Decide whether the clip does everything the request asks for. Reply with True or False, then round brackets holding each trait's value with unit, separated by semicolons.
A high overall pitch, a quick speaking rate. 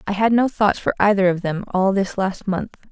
True (195 Hz; 245 wpm)